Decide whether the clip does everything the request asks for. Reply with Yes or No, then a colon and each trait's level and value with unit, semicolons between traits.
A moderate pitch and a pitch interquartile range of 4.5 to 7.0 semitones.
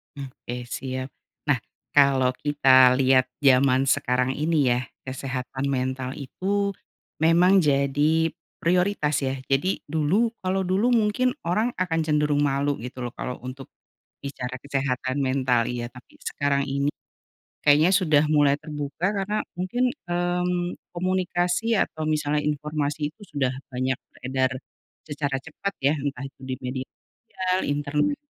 Yes: medium, 145 Hz; average, 4.9 semitones